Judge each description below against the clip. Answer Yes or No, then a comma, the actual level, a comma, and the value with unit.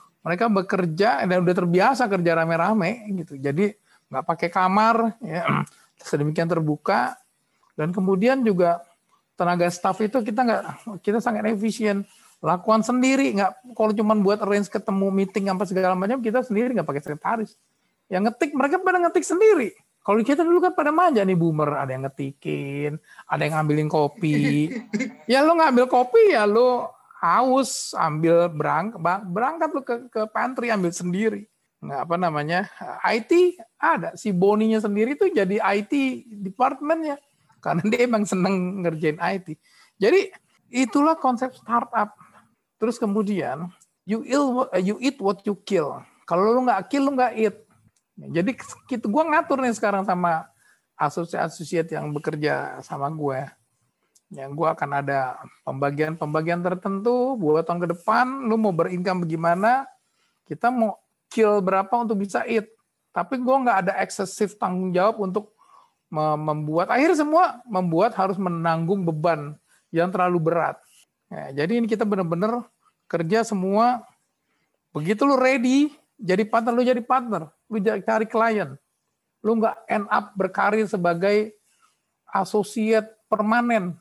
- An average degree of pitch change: No, wide, 5.7 semitones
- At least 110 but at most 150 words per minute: Yes, fast, 140 wpm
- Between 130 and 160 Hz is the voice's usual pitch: No, high, 210 Hz